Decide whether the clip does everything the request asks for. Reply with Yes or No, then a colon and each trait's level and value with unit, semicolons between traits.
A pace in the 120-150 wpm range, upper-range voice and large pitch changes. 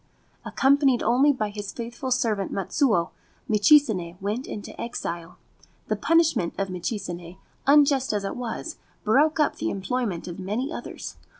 Yes: slow, 135 wpm; high, 220 Hz; wide, 5.9 semitones